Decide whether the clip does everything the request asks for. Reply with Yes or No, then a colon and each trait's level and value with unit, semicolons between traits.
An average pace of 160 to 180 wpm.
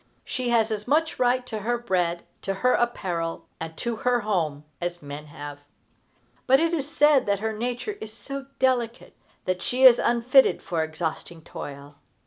Yes: average, 170 wpm